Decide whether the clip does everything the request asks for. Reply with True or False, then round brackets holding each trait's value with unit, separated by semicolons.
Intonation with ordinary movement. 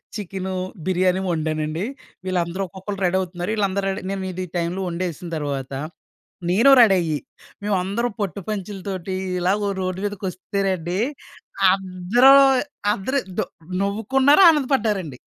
False (2.3 semitones)